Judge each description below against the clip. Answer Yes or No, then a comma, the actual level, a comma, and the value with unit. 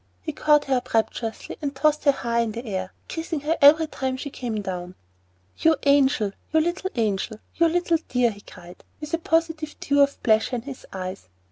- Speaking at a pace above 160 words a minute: Yes, average, 195 wpm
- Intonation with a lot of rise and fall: Yes, wide, 5.9 semitones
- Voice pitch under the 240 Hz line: No, very high, 270 Hz